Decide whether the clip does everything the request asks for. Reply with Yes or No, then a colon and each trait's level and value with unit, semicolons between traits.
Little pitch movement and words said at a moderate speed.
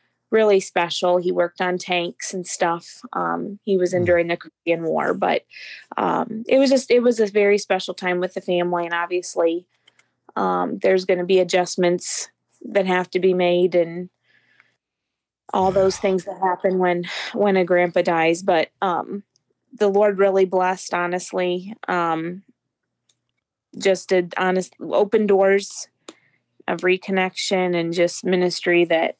Yes: narrow, 1.8 semitones; average, 150 wpm